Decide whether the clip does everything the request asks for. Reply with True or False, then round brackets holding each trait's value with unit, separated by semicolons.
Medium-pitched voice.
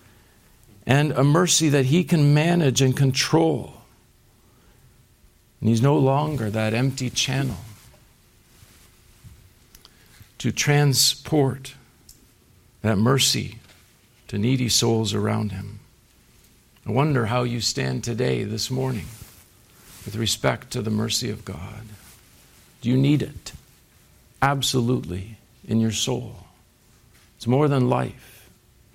False (120 Hz)